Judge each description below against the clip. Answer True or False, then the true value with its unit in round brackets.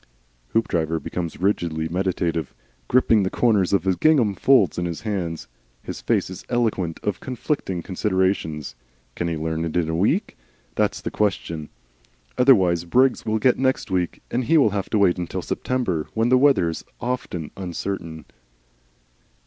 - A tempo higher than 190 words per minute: False (155 wpm)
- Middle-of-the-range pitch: False (95 Hz)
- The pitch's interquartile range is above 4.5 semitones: True (5.3 semitones)